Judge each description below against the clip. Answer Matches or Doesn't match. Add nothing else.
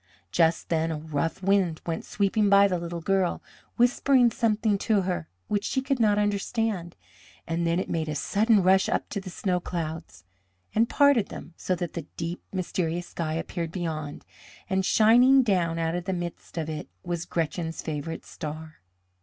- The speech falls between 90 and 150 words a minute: Doesn't match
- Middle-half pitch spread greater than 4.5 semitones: Doesn't match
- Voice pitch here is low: Doesn't match